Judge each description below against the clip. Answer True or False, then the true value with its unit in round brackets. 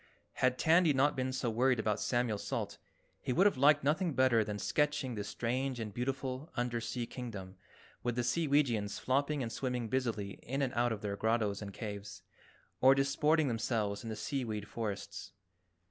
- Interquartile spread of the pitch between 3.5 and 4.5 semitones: True (3.8 semitones)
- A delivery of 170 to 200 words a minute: True (175 wpm)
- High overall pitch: False (120 Hz)